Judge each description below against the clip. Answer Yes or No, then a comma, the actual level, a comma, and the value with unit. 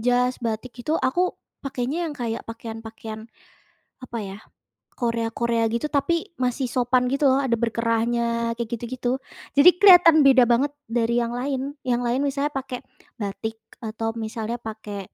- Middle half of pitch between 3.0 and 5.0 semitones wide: No, narrow, 2.5 semitones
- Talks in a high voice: Yes, high, 240 Hz